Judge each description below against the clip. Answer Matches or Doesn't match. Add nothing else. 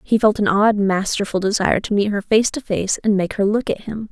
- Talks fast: Matches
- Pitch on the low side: Doesn't match